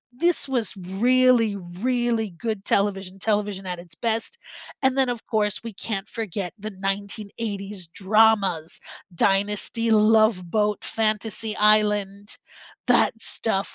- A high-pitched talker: Yes, high, 210 Hz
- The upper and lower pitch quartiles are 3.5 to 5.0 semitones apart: No, narrow, 2.4 semitones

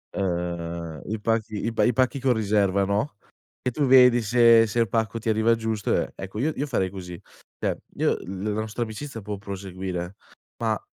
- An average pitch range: Yes, average, 3.4 semitones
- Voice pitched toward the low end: Yes, low, 110 Hz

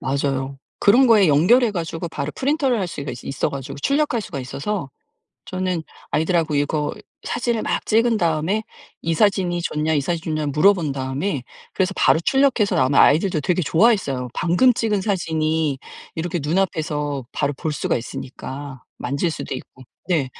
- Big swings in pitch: Yes, wide, 5.8 semitones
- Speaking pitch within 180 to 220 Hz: No, medium, 165 Hz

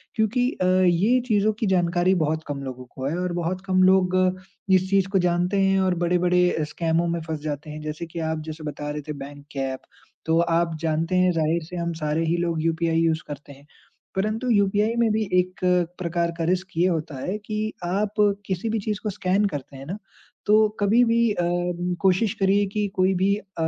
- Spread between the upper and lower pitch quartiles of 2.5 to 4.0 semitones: Yes, average, 3.5 semitones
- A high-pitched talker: No, medium, 175 Hz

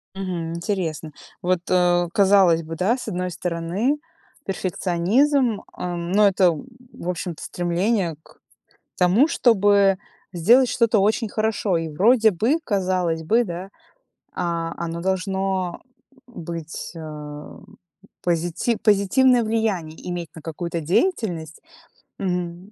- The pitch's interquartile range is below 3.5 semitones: No, average, 3.8 semitones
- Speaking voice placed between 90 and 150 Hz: No, medium, 180 Hz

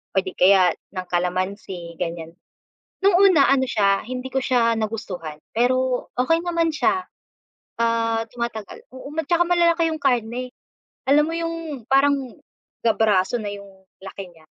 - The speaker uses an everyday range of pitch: No, wide, 6.4 semitones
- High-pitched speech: Yes, high, 235 Hz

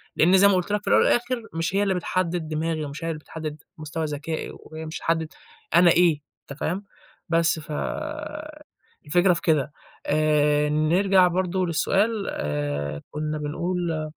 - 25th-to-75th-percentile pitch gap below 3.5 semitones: Yes, average, 3.0 semitones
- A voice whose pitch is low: No, medium, 165 Hz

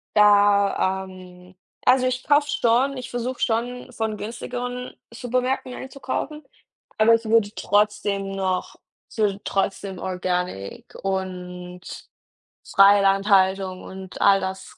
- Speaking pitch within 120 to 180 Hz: No, high, 205 Hz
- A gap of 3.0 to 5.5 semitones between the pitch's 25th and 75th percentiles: Yes, average, 4.4 semitones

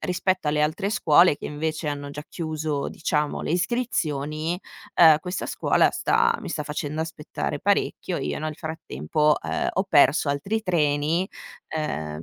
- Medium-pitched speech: Yes, medium, 155 Hz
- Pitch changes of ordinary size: Yes, average, 3.0 semitones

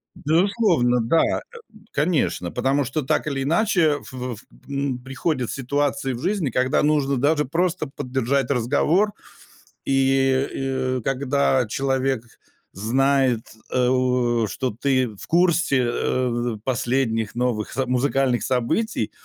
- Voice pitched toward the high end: No, low, 135 Hz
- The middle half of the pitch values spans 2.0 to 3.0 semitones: Yes, average, 2.7 semitones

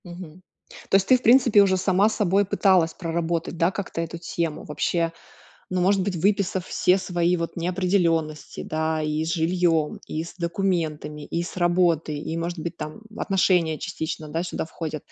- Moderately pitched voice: Yes, medium, 170 Hz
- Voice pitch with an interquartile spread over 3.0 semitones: No, narrow, 2.5 semitones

